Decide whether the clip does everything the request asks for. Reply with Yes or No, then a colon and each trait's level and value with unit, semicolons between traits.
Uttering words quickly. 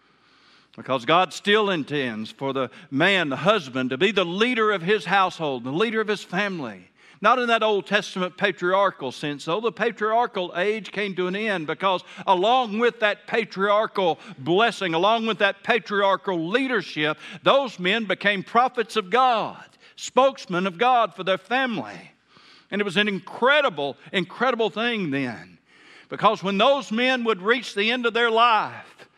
No: average, 160 wpm